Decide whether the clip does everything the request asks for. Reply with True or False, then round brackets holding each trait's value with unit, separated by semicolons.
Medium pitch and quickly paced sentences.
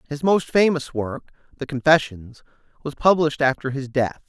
False (145 Hz; 155 wpm)